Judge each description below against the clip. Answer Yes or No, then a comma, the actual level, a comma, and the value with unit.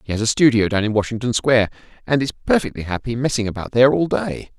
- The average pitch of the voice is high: No, low, 120 Hz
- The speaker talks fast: Yes, fast, 220 wpm